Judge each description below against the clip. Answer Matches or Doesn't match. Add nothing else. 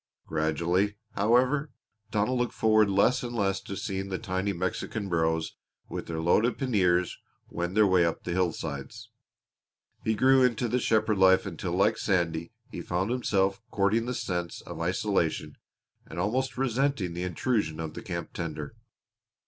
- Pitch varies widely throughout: Doesn't match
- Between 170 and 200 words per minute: Doesn't match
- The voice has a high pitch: Doesn't match